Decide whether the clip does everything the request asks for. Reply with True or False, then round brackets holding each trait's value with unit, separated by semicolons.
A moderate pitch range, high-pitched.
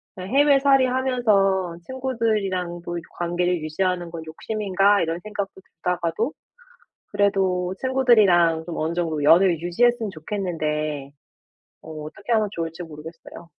False (4.2 semitones; 180 Hz)